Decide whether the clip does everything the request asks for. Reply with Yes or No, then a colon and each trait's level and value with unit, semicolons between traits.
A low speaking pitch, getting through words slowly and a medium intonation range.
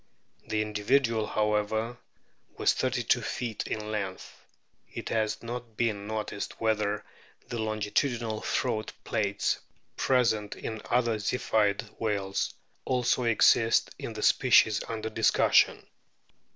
No: low, 110 Hz; slow, 115 wpm; narrow, 1.6 semitones